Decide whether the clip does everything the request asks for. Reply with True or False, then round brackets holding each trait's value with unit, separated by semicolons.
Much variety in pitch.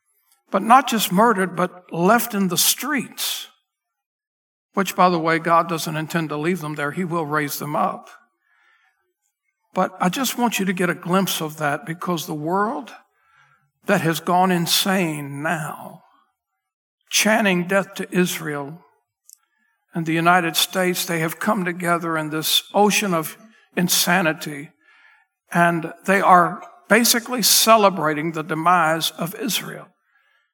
False (4.3 semitones)